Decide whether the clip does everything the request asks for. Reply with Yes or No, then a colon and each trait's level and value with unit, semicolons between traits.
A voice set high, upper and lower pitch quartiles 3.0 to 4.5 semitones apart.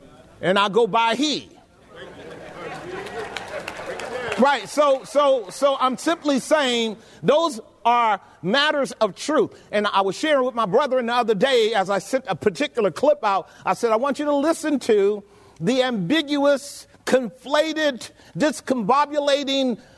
No: very high, 255 Hz; average, 4.9 semitones